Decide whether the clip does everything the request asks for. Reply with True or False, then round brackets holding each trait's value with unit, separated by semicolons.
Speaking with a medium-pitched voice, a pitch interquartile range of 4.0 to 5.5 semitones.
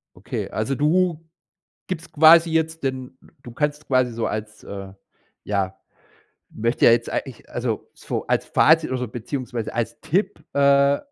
False (130 Hz; 4.8 semitones)